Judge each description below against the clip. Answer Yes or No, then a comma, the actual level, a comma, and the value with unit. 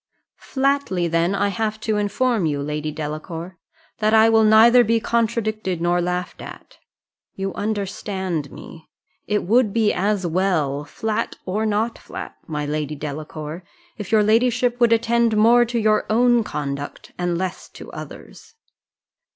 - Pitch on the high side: Yes, high, 205 Hz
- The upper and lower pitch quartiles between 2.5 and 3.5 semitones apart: No, average, 4.9 semitones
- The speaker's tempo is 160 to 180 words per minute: No, average, 145 wpm